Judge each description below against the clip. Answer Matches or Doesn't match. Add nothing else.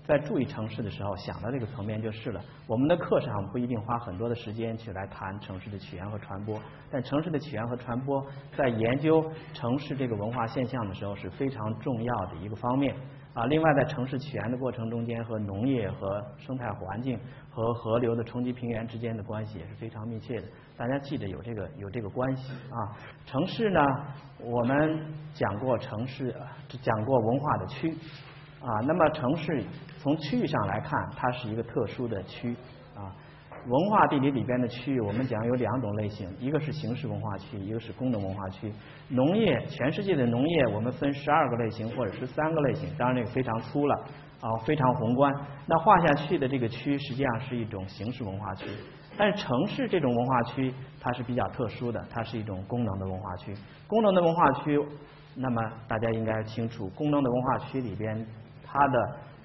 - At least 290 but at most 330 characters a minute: Matches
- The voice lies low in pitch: Matches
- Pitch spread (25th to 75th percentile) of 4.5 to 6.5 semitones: Doesn't match